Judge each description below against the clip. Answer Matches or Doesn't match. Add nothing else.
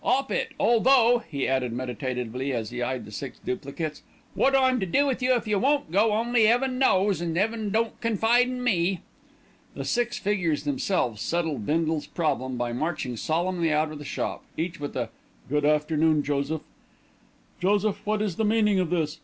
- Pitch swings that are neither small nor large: Doesn't match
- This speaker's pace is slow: Doesn't match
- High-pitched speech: Doesn't match